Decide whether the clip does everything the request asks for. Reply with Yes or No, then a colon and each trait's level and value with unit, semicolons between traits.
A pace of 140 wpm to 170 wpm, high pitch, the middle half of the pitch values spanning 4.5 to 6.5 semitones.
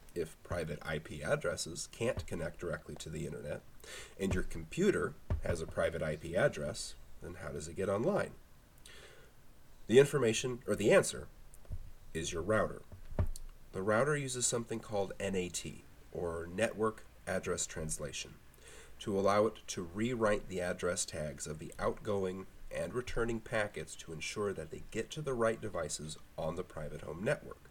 No: average, 150 wpm; low, 105 Hz; wide, 5.5 semitones